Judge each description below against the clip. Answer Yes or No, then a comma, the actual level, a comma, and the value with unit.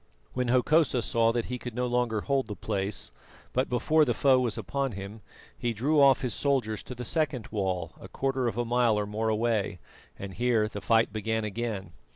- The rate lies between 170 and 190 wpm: No, average, 200 wpm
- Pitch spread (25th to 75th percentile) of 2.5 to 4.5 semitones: Yes, average, 2.9 semitones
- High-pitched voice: No, low, 120 Hz